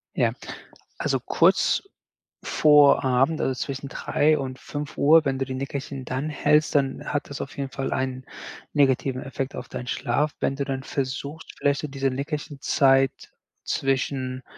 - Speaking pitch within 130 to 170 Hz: Yes, low, 135 Hz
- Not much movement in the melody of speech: Yes, narrow, 1.6 semitones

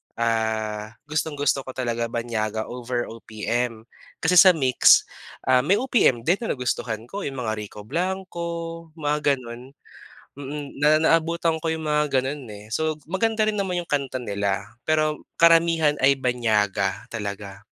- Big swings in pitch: Yes, wide, 5.9 semitones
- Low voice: Yes, low, 130 Hz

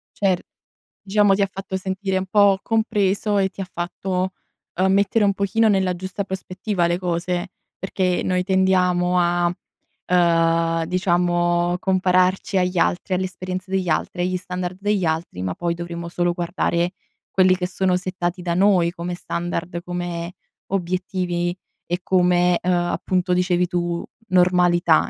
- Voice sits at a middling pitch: Yes, medium, 180 Hz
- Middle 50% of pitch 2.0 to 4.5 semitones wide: No, narrow, 1.5 semitones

